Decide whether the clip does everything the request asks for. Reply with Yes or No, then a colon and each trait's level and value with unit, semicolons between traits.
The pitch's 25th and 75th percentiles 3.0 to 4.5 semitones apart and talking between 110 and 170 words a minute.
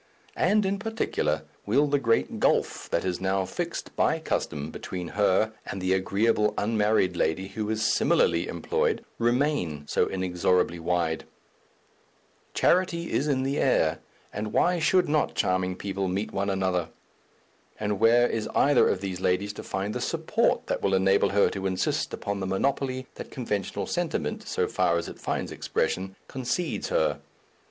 No: wide, 5.4 semitones; average, 160 wpm